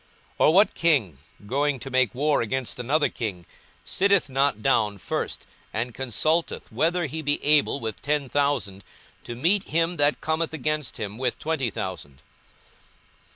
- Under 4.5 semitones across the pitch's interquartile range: No, average, 5.2 semitones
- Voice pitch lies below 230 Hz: Yes, medium, 140 Hz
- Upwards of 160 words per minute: No, average, 155 wpm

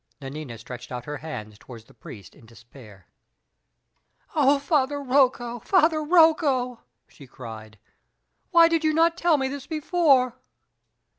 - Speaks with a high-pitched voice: Yes, very high, 255 Hz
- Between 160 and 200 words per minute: No, slow, 135 wpm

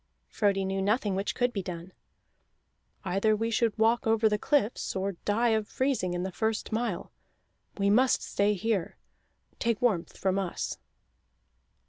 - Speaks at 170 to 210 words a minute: No, average, 150 wpm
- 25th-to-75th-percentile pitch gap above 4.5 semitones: No, average, 2.9 semitones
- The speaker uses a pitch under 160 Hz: No, high, 210 Hz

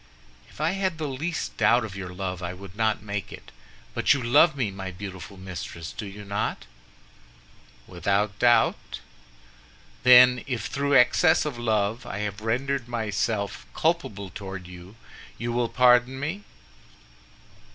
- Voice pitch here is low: Yes, low, 110 Hz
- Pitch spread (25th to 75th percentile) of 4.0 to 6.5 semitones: Yes, average, 4.6 semitones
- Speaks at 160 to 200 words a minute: No, average, 145 wpm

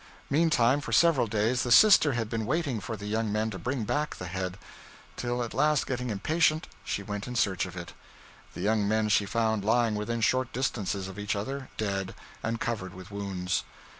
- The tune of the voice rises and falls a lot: No, average, 3.9 semitones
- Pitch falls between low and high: No, low, 110 Hz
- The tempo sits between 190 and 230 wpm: Yes, average, 195 wpm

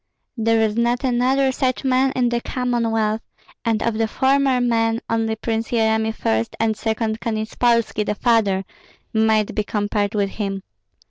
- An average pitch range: No, narrow, 1.9 semitones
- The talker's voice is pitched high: Yes, high, 225 Hz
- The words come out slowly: No, average, 150 wpm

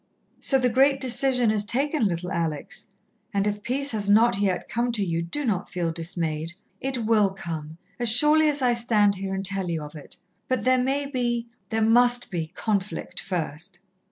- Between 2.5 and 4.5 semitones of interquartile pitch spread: No, wide, 5.6 semitones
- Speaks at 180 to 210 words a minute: Yes, average, 185 wpm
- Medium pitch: No, high, 210 Hz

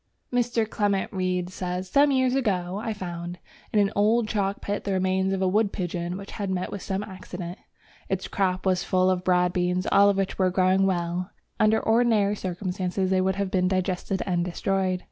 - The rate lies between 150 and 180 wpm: No, average, 200 wpm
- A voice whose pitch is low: No, high, 190 Hz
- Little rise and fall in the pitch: Yes, narrow, 1.8 semitones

